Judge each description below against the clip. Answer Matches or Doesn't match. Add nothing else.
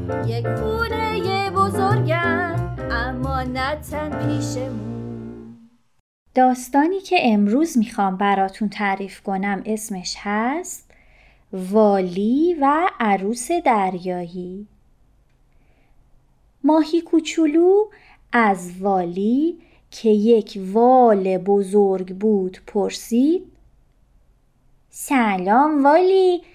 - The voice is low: Doesn't match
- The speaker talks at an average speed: Doesn't match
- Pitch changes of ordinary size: Doesn't match